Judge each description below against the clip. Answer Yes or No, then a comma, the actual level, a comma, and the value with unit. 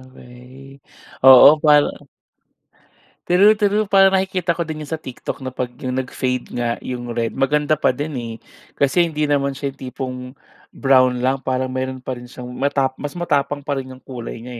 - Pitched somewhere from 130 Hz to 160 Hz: Yes, low, 135 Hz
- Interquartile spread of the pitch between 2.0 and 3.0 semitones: Yes, average, 2.7 semitones